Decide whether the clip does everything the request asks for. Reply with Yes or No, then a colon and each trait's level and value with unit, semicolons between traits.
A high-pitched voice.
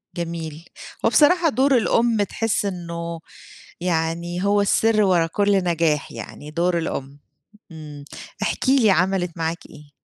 No: medium, 175 Hz